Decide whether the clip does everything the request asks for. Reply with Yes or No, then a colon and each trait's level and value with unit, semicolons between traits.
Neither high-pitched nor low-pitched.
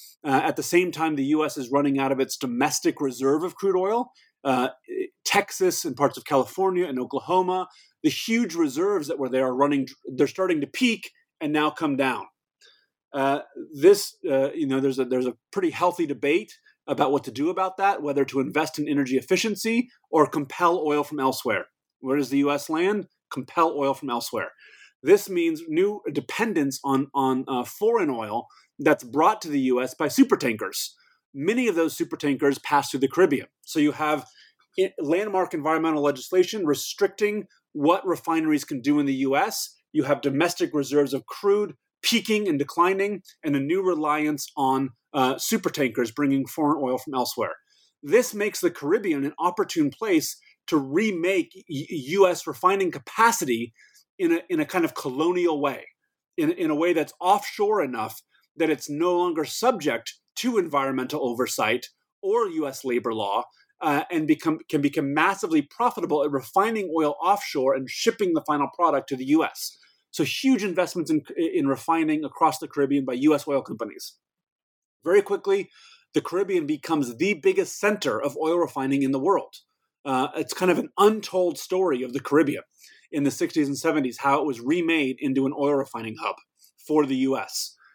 Yes: medium, 170 Hz